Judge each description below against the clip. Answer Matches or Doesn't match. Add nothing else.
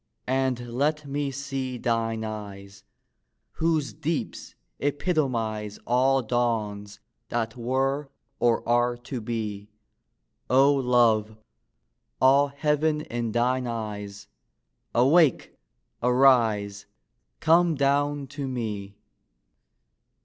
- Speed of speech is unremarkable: Doesn't match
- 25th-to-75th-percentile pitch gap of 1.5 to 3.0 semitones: Doesn't match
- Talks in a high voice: Doesn't match